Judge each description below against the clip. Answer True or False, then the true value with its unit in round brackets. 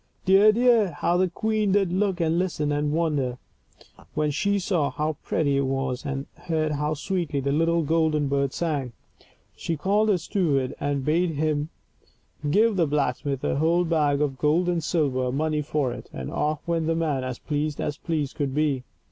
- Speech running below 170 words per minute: False (180 wpm)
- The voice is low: False (155 Hz)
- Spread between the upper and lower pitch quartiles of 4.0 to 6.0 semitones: False (3.3 semitones)